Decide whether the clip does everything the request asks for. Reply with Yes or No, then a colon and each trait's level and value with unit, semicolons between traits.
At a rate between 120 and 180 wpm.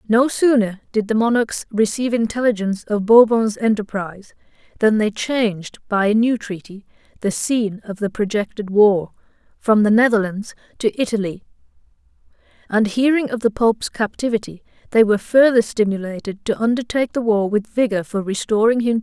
Yes: average, 155 wpm